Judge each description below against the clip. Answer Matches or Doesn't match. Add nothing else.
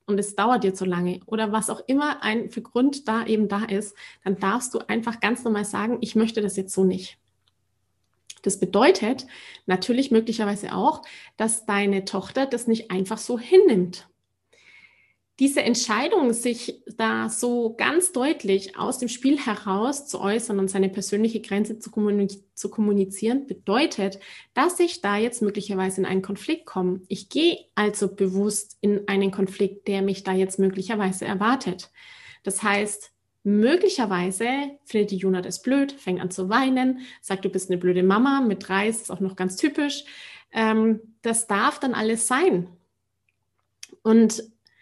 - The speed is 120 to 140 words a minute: Doesn't match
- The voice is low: Doesn't match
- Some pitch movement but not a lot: Matches